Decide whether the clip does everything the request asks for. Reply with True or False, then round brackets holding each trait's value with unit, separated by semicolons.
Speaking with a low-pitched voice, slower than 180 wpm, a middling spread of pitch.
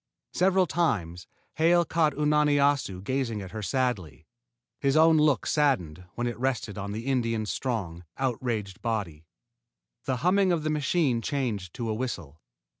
False (125 Hz; 155 wpm; 6.6 semitones)